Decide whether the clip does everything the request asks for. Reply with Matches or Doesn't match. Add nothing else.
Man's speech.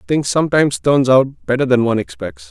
Matches